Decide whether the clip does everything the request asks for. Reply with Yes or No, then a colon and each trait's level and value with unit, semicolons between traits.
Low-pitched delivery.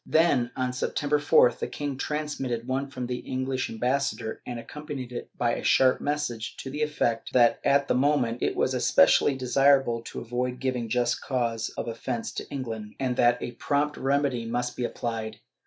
Yes: low, 125 Hz